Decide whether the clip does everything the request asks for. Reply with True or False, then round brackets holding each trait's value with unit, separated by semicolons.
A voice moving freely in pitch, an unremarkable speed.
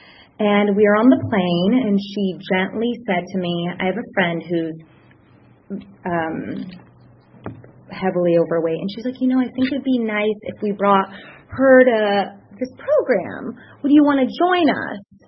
True (5.8 semitones; 170 wpm)